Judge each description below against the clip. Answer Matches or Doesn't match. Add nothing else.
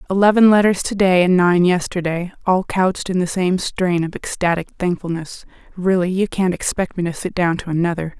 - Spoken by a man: Doesn't match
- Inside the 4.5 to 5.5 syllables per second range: Matches